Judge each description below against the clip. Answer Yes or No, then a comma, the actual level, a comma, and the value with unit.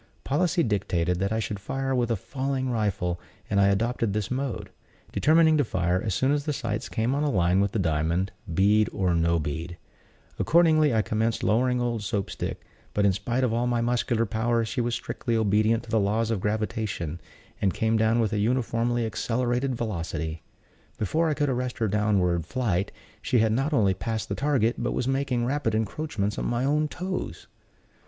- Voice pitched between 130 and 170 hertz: No, low, 115 Hz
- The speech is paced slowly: No, average, 190 wpm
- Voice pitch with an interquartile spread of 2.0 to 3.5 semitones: No, average, 4.2 semitones